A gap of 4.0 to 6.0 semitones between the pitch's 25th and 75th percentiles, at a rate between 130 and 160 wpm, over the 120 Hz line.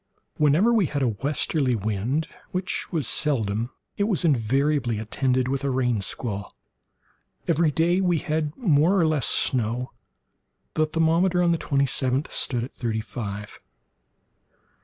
Yes: average, 5.3 semitones; average, 140 wpm; medium, 140 Hz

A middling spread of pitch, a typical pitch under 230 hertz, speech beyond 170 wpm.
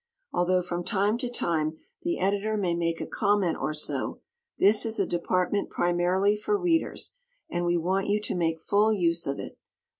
Yes: average, 3.3 semitones; medium, 185 Hz; average, 180 wpm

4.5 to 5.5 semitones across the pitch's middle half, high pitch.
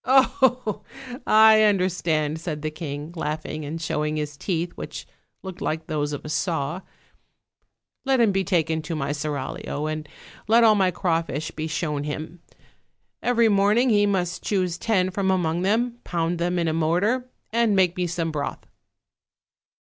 No: average, 4.8 semitones; medium, 175 Hz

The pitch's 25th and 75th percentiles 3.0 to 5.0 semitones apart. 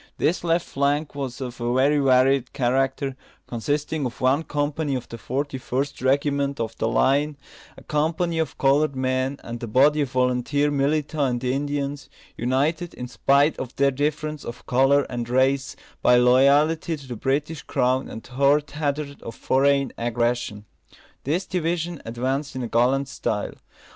No: narrow, 2.5 semitones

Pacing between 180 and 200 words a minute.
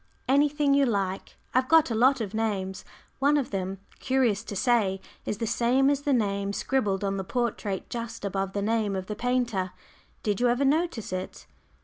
Yes: average, 190 wpm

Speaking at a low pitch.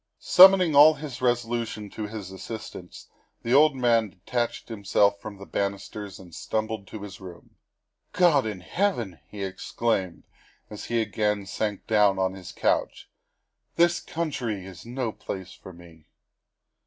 Yes: low, 110 Hz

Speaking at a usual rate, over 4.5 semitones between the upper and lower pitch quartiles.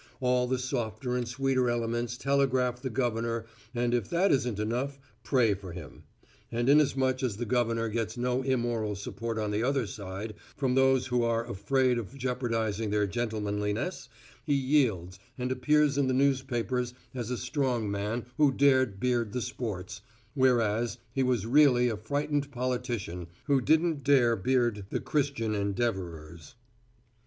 No: average, 150 wpm; average, 3.1 semitones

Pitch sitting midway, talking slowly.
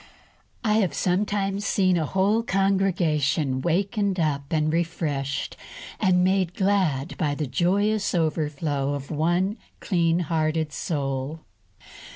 Yes: medium, 170 Hz; slow, 115 wpm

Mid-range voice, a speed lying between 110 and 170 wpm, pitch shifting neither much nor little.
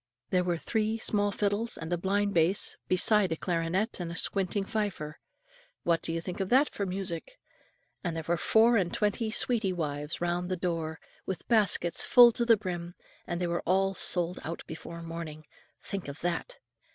No: medium, 180 Hz; average, 185 wpm; average, 3.5 semitones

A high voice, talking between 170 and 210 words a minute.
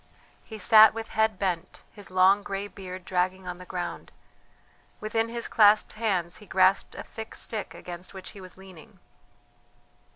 No: high, 195 Hz; average, 160 wpm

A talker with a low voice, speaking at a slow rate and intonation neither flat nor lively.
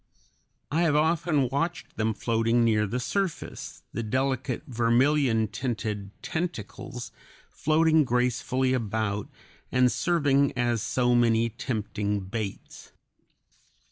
Yes: low, 120 Hz; slow, 105 wpm; average, 4.1 semitones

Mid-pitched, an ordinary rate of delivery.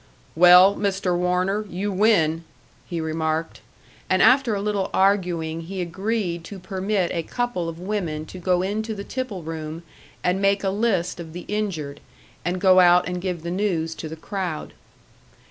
Yes: medium, 180 Hz; average, 165 wpm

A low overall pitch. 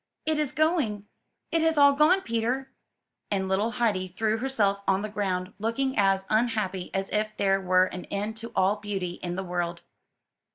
No: high, 210 Hz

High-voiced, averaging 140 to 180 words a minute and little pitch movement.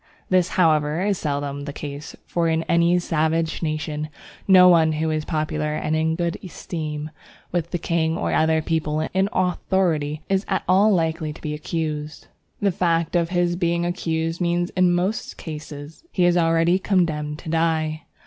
No: medium, 165 Hz; average, 170 wpm; narrow, 2.2 semitones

